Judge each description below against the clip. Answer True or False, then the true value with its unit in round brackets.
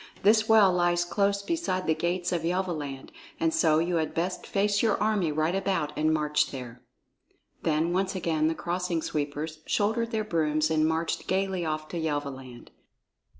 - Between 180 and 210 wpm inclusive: False (165 wpm)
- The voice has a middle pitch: True (170 Hz)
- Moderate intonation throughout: True (3.7 semitones)